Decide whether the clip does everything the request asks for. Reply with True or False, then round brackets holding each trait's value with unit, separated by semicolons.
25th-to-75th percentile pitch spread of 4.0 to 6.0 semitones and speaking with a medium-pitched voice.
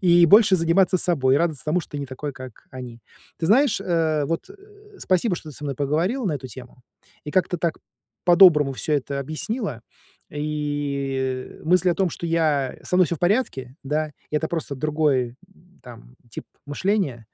True (4.3 semitones; 155 Hz)